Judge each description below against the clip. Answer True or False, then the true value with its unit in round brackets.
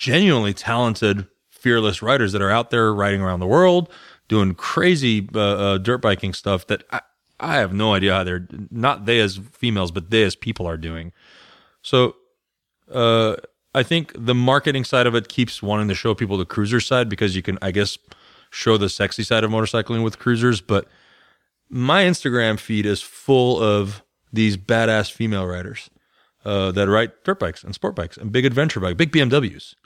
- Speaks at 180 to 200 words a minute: True (185 wpm)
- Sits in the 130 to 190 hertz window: False (110 Hz)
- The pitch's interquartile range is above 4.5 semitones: False (3.5 semitones)